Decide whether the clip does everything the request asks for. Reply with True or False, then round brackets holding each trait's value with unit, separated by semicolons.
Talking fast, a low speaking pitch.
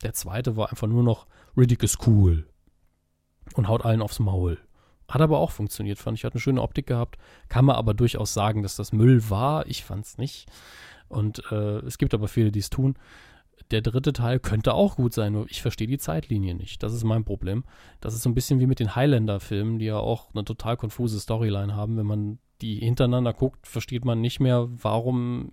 True (210 wpm; 115 Hz)